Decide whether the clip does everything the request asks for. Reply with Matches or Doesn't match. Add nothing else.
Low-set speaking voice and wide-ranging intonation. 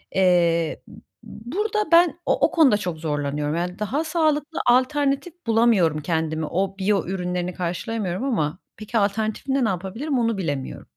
Doesn't match